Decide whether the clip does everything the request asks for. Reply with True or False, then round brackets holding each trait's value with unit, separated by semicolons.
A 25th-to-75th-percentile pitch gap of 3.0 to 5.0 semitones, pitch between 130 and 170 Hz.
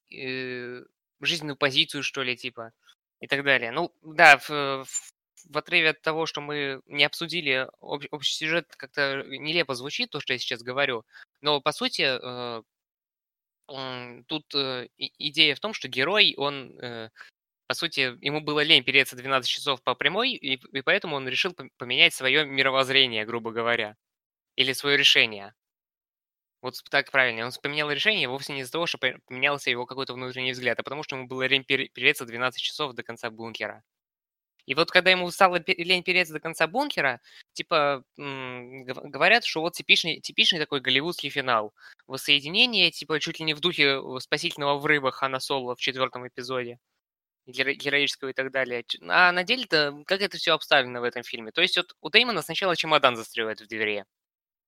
True (3.5 semitones; 140 Hz)